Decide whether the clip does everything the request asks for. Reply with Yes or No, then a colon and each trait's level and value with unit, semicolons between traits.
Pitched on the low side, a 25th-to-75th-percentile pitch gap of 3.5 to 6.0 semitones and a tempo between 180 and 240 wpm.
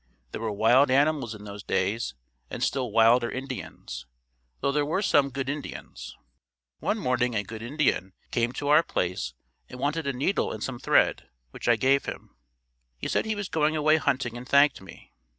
Yes: low, 130 Hz; average, 4.4 semitones; average, 185 wpm